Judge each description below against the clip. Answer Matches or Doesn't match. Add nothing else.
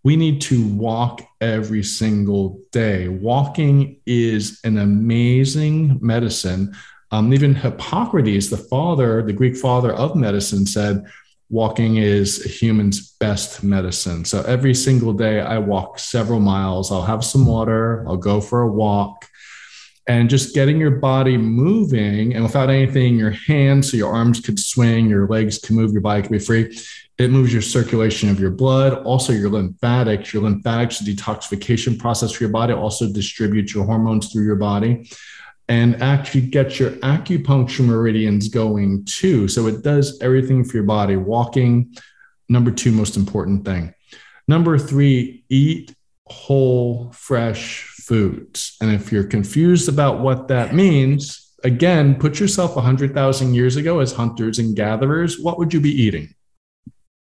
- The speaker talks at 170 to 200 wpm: Doesn't match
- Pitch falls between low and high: Doesn't match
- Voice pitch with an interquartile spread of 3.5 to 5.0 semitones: Matches